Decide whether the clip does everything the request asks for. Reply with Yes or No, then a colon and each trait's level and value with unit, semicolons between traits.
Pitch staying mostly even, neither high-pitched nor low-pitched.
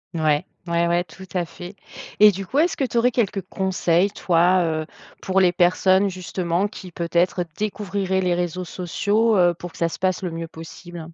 Yes: narrow, 2.2 semitones; medium, 180 Hz